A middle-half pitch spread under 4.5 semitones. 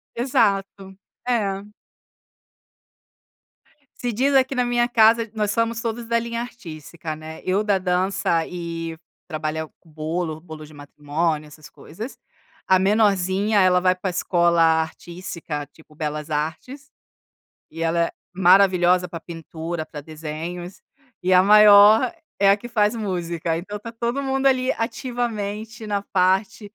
No: average, 5.1 semitones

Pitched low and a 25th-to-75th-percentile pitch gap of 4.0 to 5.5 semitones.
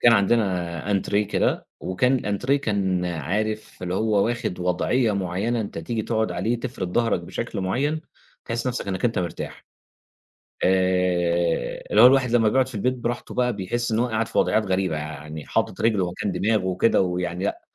Yes: low, 100 Hz; average, 4.4 semitones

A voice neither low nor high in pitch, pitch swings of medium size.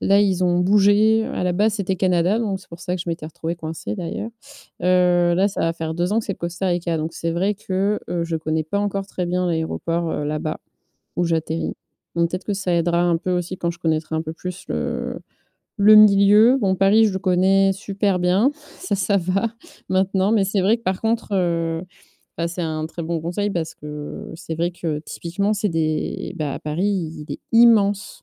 Yes: medium, 180 Hz; average, 3.1 semitones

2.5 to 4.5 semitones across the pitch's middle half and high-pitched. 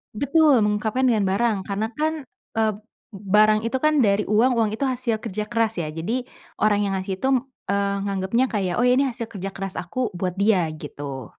Yes: average, 3.8 semitones; high, 215 Hz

